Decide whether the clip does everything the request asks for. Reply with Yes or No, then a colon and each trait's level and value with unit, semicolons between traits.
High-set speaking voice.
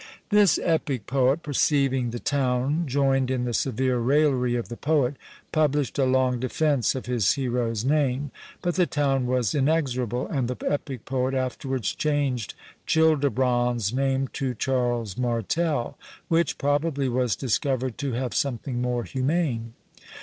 No: low, 130 Hz